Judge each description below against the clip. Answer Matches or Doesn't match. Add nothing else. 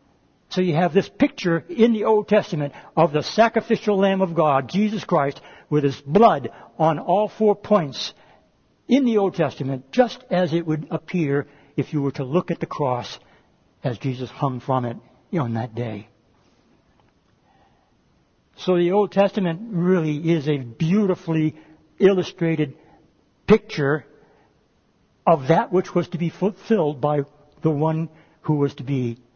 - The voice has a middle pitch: Matches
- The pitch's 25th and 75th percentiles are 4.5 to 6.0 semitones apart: Matches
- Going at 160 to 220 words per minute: Doesn't match